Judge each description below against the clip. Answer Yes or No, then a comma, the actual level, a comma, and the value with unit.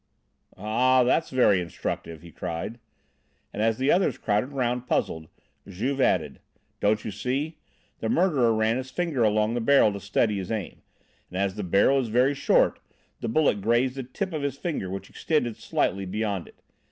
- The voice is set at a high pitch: No, low, 115 Hz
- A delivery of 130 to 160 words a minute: No, average, 175 wpm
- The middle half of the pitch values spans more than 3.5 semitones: Yes, average, 4.7 semitones